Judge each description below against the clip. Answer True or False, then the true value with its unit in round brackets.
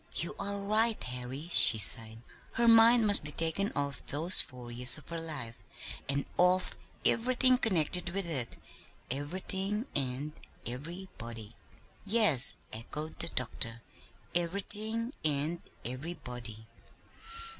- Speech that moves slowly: True (115 wpm)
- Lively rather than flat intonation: True (7.8 semitones)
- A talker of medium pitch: True (160 Hz)